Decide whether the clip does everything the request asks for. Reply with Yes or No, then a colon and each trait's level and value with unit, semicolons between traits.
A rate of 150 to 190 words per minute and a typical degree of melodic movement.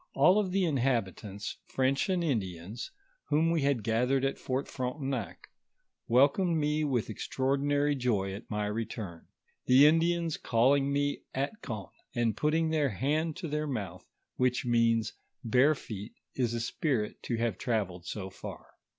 No: average, 140 wpm; average, 4.8 semitones